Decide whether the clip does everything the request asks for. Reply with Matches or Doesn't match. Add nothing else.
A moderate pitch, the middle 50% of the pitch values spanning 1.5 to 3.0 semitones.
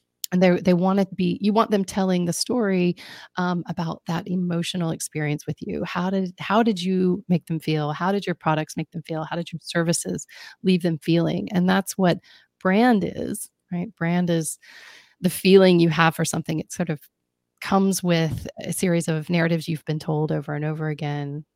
Matches